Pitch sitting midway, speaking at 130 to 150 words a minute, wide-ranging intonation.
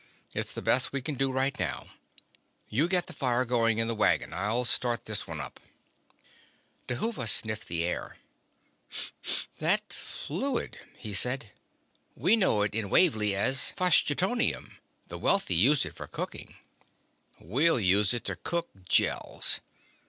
No: low, 125 Hz; average, 145 wpm; wide, 6.0 semitones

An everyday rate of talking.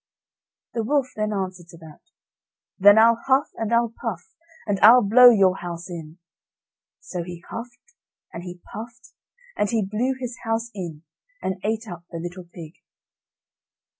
Yes: average, 155 wpm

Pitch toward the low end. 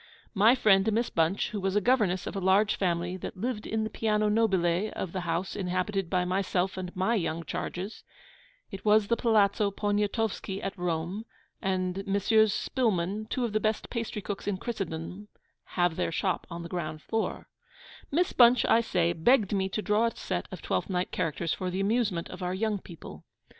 No: high, 195 Hz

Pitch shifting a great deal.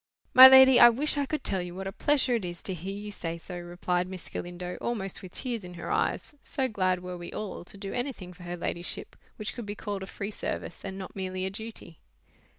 No: average, 4.2 semitones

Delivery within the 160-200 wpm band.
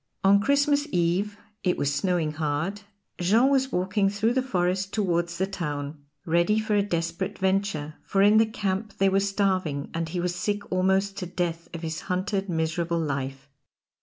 Yes: average, 170 wpm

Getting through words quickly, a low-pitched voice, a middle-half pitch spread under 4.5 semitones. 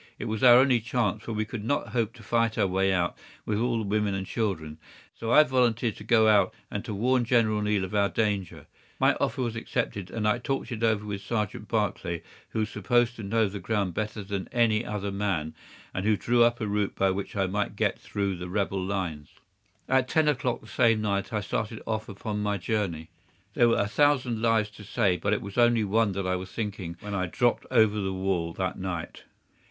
Yes: fast, 225 wpm; low, 105 Hz; average, 2.9 semitones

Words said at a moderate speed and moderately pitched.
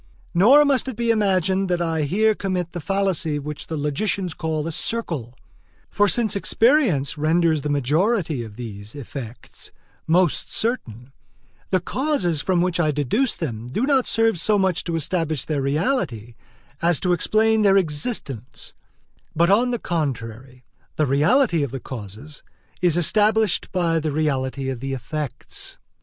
Yes: average, 150 wpm; medium, 165 Hz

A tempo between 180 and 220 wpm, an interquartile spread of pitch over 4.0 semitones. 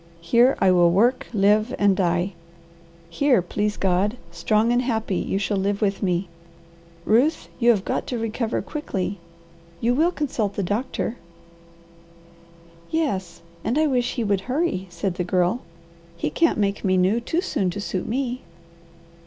No: average, 155 wpm; average, 4.7 semitones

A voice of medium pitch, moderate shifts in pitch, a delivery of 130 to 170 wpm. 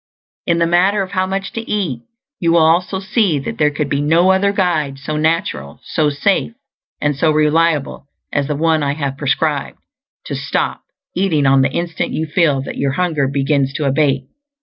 No: medium, 155 Hz; average, 3.8 semitones; average, 190 wpm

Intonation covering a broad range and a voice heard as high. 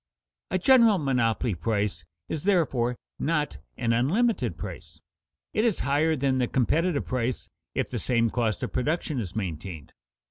No: wide, 6.4 semitones; low, 125 Hz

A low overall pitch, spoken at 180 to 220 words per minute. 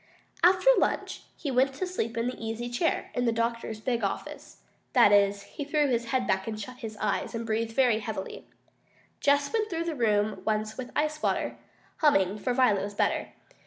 No: high, 235 Hz; average, 195 wpm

